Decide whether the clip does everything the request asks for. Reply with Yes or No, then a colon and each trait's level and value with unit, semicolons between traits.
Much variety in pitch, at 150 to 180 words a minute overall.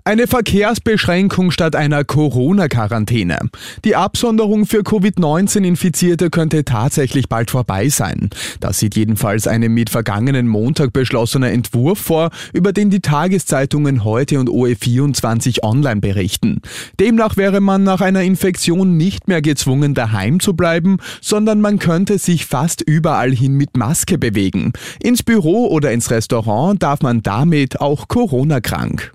No: wide, 7.4 semitones; average, 135 wpm